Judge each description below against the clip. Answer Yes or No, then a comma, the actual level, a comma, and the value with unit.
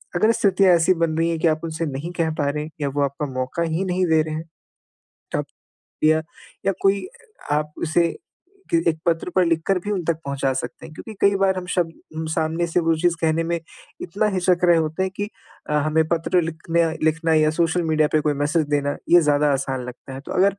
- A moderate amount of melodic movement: No, narrow, 2.3 semitones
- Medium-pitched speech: Yes, medium, 165 Hz